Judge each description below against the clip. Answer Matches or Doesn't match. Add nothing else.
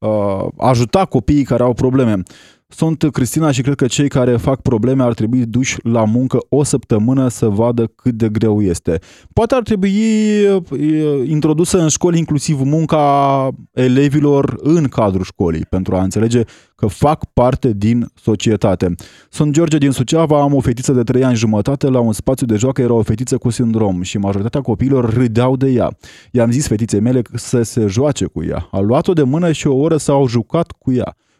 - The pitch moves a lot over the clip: Doesn't match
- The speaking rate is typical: Doesn't match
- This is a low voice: Matches